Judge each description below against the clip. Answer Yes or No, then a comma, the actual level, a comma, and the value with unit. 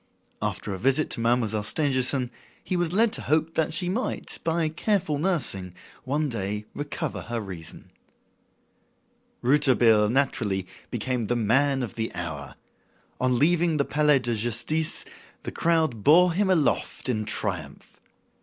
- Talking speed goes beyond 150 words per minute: No, average, 140 wpm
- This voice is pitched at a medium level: No, low, 130 Hz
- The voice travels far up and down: Yes, wide, 6.3 semitones